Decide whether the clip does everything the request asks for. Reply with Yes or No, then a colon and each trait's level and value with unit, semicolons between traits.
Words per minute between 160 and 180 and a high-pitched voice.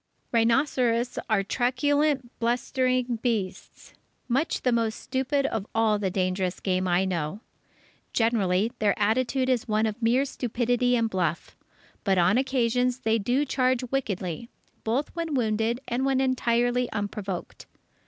No: slow, 135 wpm; high, 235 Hz